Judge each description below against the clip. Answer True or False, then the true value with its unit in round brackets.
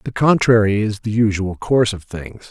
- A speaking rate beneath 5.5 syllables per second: True (5.0 syllables/s)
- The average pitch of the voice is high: False (110 Hz)